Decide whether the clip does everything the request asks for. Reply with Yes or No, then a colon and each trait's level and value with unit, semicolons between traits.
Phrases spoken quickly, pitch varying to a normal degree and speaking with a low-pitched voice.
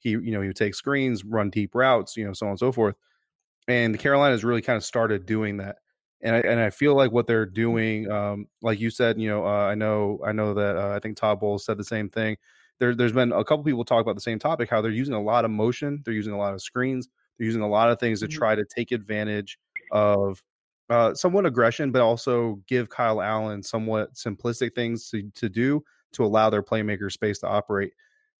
No: fast, 240 wpm; narrow, 2.3 semitones; low, 110 Hz